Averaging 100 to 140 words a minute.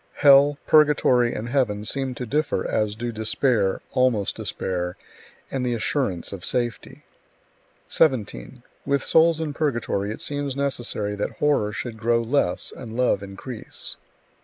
Yes: slow, 135 wpm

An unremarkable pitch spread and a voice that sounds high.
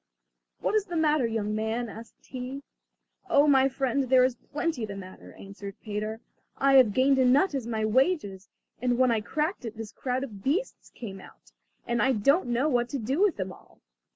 Yes: average, 4.2 semitones; very high, 250 Hz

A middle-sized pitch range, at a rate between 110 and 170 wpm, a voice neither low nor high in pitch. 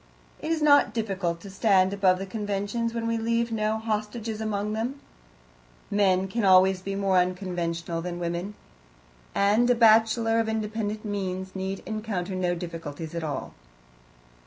No: average, 3.2 semitones; average, 150 wpm; high, 200 Hz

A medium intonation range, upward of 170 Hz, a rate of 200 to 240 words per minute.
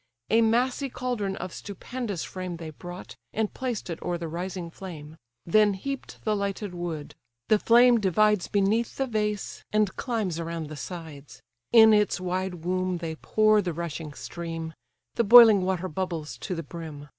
No: average, 4.2 semitones; medium, 185 Hz; average, 165 wpm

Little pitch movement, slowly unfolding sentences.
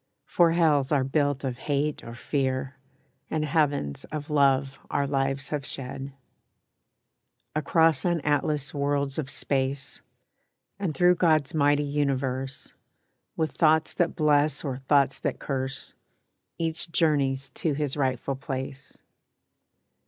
Yes: narrow, 2.2 semitones; slow, 120 wpm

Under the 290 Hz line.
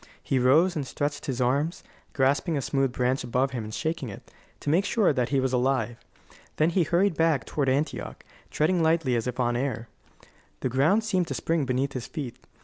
Yes: low, 135 Hz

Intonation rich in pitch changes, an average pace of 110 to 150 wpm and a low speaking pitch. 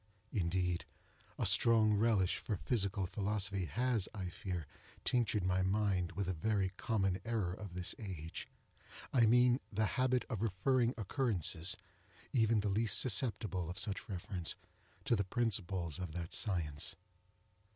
No: average, 3.7 semitones; slow, 135 wpm; low, 100 Hz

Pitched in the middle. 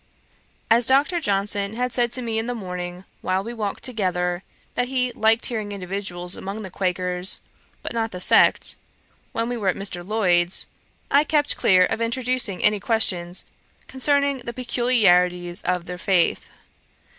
No: high, 205 Hz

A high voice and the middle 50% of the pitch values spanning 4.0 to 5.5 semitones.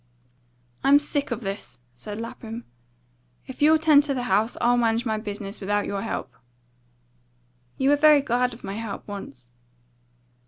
Yes: high, 230 Hz; average, 5.0 semitones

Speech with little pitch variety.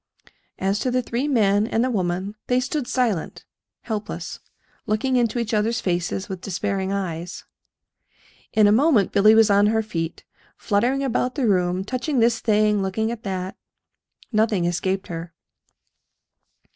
No: average, 3.7 semitones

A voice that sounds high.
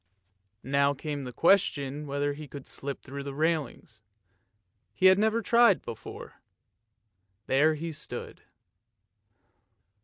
No: medium, 145 Hz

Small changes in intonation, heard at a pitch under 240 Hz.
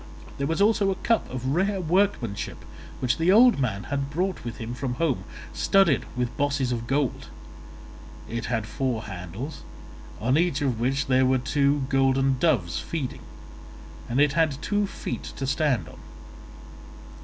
No: average, 4.9 semitones; low, 135 Hz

